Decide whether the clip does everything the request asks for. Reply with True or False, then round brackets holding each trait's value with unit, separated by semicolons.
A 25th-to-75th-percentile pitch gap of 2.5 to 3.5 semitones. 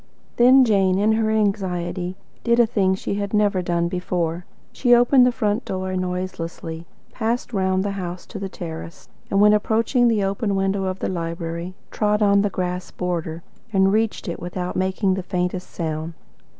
True (2.9 semitones)